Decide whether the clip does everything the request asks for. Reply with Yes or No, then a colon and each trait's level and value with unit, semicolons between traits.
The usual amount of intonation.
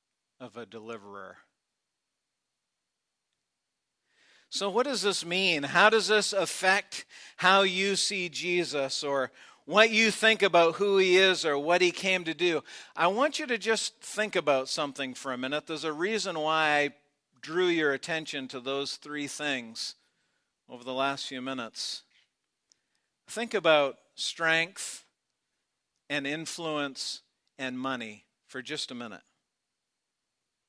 No: wide, 6.1 semitones